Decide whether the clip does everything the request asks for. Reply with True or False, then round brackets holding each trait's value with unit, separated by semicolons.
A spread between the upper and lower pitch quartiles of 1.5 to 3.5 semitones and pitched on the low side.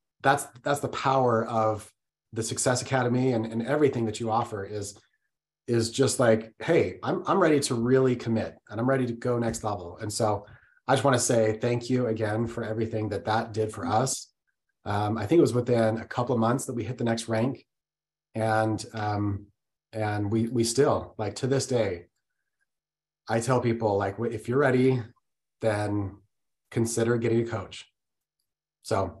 True (2.9 semitones; 115 Hz)